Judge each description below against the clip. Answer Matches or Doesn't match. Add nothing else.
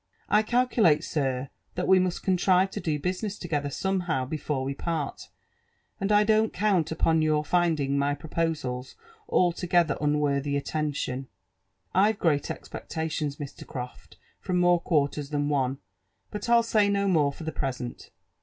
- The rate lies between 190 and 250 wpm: Doesn't match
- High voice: Doesn't match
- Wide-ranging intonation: Doesn't match